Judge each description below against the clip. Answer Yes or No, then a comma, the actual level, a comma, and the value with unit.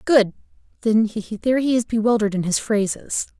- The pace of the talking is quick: No, average, 140 wpm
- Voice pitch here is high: Yes, high, 220 Hz